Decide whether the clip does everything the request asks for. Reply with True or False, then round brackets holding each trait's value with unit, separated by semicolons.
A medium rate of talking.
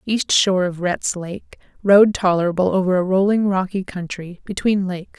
True (150 wpm)